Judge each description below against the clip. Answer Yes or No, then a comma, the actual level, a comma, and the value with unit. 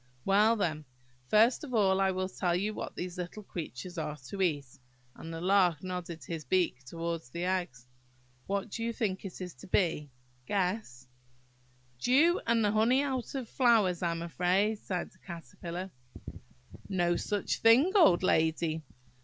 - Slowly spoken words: No, average, 160 wpm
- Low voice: No, medium, 185 Hz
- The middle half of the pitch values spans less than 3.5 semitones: No, average, 4.0 semitones